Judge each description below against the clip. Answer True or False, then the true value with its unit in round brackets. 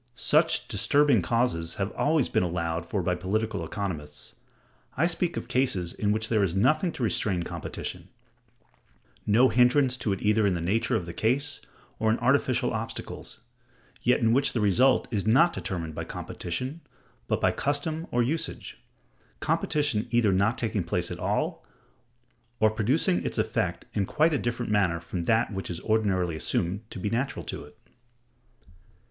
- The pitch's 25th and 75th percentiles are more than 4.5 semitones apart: True (5.4 semitones)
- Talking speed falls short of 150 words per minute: False (165 wpm)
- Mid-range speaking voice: False (110 Hz)